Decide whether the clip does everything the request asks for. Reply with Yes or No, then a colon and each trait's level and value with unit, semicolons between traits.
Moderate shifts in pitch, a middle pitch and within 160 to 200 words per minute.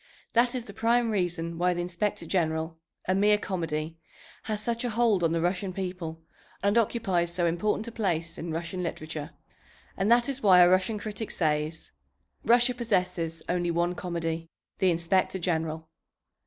Yes: average, 4.1 semitones; medium, 180 Hz; average, 165 wpm